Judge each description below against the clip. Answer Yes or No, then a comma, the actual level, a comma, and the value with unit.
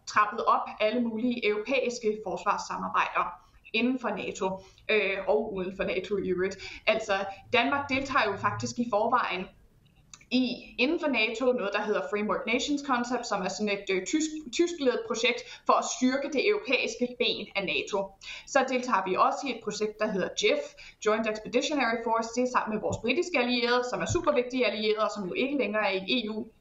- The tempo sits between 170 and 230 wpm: Yes, average, 185 wpm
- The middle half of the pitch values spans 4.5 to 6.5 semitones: No, average, 3.9 semitones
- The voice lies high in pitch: Yes, high, 225 Hz